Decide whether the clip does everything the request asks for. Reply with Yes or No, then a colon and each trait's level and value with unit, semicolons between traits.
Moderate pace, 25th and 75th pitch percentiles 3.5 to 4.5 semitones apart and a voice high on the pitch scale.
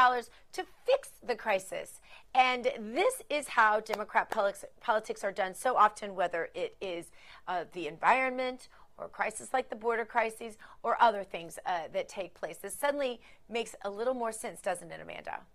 Yes: average, 165 wpm; average, 4.1 semitones; high, 230 Hz